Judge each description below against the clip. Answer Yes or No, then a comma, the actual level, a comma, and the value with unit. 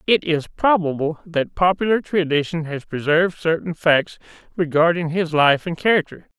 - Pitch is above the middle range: No, medium, 165 Hz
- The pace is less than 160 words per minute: Yes, average, 140 wpm